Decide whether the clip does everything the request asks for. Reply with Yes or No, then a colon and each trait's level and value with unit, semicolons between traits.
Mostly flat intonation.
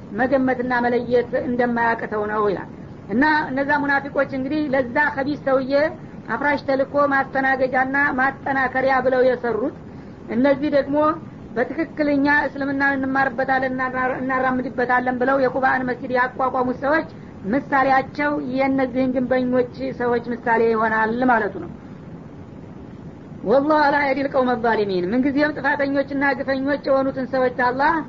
Yes: narrow, 1.9 semitones